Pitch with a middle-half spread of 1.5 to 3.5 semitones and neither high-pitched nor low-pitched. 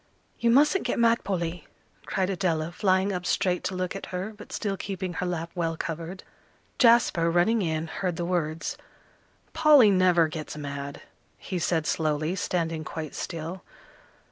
Yes: average, 3.1 semitones; medium, 180 Hz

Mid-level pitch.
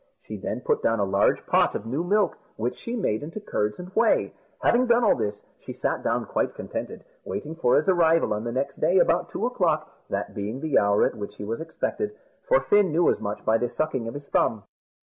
Yes: medium, 150 Hz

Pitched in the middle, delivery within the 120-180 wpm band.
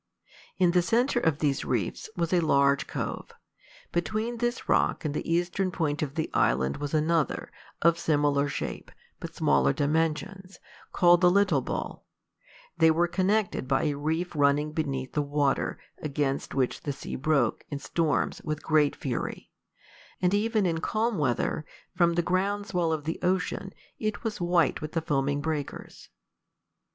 Yes: medium, 160 Hz; average, 160 wpm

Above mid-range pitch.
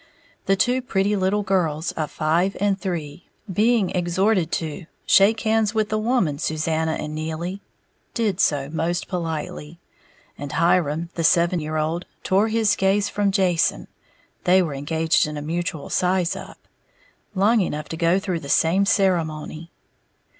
No: medium, 175 Hz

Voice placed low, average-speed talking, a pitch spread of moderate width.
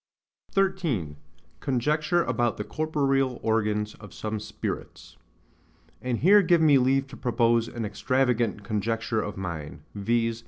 No: low, 120 Hz; slow, 125 wpm; average, 4.2 semitones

